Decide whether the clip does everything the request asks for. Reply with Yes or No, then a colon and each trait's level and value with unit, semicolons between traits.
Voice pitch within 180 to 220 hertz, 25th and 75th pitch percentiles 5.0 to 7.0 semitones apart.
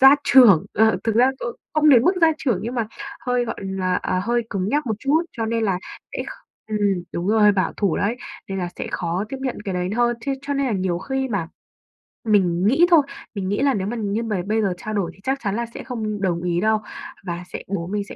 No: high, 215 Hz; average, 4.2 semitones